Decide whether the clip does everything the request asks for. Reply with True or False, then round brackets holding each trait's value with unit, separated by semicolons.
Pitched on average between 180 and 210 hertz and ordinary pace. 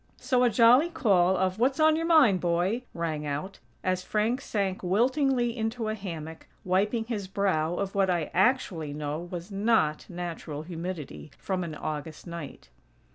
True (190 Hz; 160 wpm)